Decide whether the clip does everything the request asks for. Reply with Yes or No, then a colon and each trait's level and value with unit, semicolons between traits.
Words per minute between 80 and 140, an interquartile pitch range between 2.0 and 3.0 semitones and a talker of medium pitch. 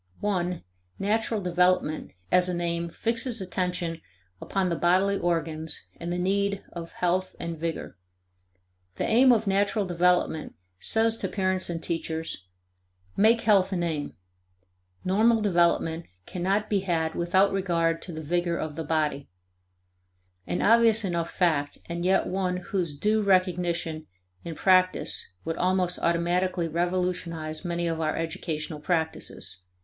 Yes: slow, 135 wpm; narrow, 2.5 semitones; medium, 175 Hz